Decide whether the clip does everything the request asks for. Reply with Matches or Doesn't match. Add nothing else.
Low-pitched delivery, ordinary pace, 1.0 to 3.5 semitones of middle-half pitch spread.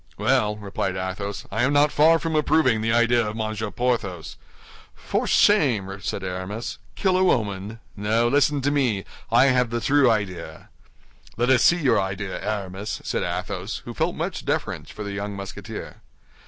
Doesn't match